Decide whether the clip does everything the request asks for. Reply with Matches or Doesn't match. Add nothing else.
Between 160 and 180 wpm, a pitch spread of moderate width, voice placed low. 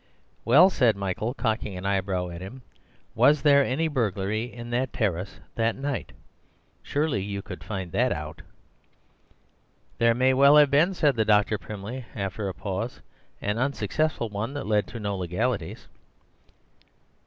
Doesn't match